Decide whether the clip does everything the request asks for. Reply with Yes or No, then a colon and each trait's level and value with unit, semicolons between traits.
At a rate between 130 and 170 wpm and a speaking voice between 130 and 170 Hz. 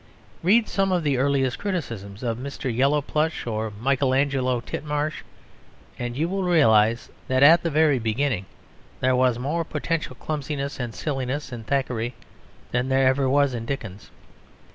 Yes: average, 150 wpm; low, 135 Hz